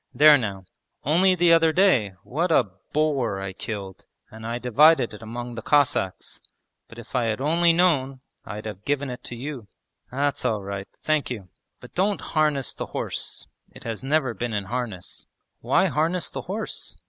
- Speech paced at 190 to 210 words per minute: No, average, 175 wpm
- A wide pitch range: Yes, wide, 5.9 semitones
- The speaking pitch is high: No, low, 130 Hz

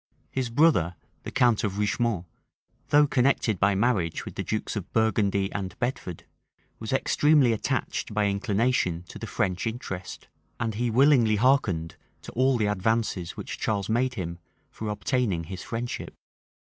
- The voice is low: Yes, low, 110 Hz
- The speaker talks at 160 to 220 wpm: No, average, 150 wpm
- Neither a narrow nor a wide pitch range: Yes, average, 4.2 semitones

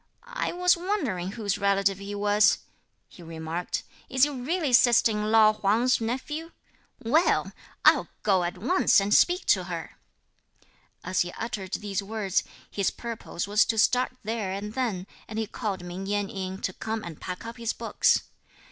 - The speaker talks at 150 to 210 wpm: Yes, average, 165 wpm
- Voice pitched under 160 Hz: No, high, 210 Hz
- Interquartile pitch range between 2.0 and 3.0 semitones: No, average, 3.8 semitones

